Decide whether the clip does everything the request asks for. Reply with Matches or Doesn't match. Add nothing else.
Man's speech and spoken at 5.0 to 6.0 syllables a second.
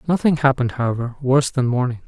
Doesn't match